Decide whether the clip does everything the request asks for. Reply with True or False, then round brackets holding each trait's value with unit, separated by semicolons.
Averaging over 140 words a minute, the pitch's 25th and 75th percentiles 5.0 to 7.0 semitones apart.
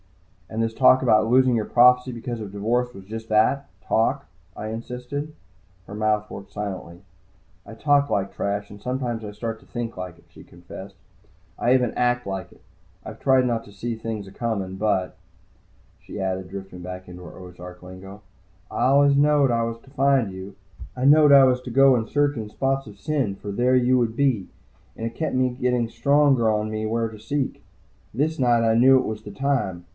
False (195 wpm; 4.1 semitones)